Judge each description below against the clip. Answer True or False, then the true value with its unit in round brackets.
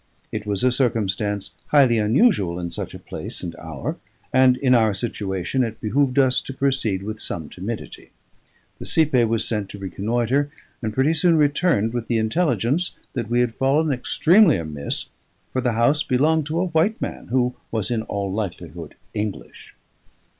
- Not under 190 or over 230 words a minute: False (170 wpm)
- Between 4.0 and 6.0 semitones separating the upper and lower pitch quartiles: True (5.2 semitones)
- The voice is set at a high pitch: False (120 Hz)